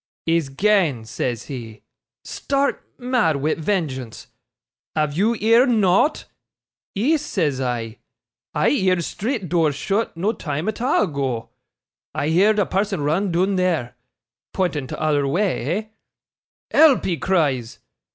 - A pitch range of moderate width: No, wide, 6.8 semitones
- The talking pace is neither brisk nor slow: No, slow, 130 wpm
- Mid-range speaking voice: Yes, medium, 175 Hz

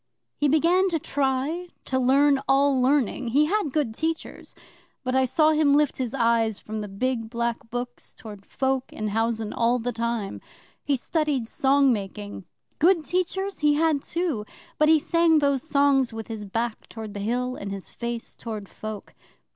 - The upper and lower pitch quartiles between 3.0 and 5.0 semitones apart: Yes, average, 4.6 semitones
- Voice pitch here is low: No, very high, 260 Hz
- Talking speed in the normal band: Yes, average, 170 wpm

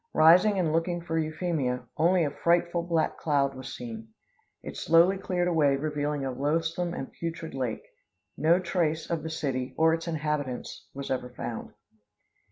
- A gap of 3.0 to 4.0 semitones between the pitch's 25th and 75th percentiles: Yes, average, 3.6 semitones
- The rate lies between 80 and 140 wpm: No, average, 160 wpm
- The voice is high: No, medium, 160 Hz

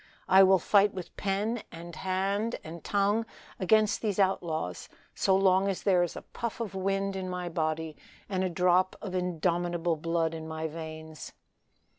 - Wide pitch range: No, average, 2.9 semitones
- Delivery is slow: No, average, 165 wpm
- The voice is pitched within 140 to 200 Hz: Yes, medium, 185 Hz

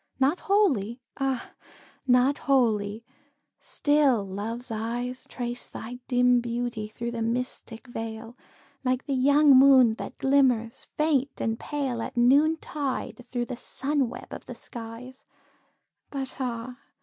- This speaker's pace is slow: Yes, slow, 125 wpm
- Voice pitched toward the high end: Yes, very high, 250 Hz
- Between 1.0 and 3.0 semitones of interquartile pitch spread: Yes, average, 2.7 semitones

